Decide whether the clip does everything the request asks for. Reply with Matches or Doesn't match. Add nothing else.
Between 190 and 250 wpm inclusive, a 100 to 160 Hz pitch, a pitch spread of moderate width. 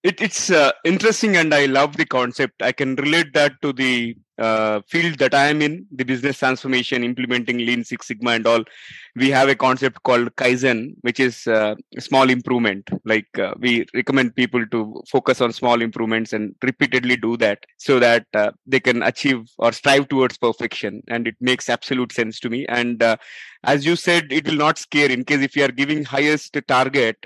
Matches